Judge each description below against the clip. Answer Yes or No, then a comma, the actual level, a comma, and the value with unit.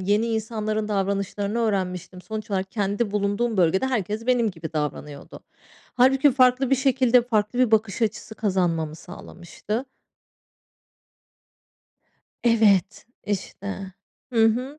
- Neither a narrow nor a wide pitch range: Yes, average, 3.6 semitones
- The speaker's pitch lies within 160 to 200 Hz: No, high, 215 Hz